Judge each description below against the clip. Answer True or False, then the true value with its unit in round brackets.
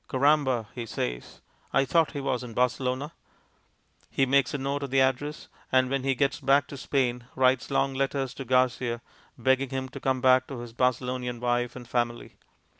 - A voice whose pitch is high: False (130 Hz)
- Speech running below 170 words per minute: False (185 wpm)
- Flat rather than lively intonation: True (1.7 semitones)